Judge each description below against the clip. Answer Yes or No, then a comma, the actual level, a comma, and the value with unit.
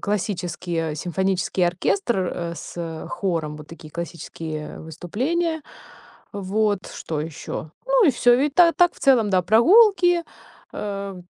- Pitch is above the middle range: Yes, high, 195 Hz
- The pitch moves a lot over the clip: Yes, wide, 7.8 semitones